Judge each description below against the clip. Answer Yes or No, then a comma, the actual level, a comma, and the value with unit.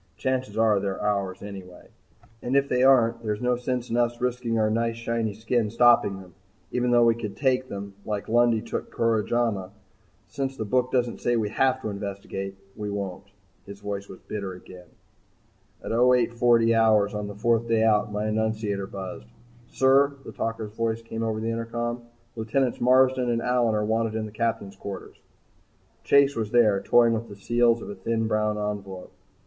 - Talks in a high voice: No, low, 115 Hz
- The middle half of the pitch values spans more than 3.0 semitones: No, narrow, 2.6 semitones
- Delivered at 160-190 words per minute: Yes, average, 180 wpm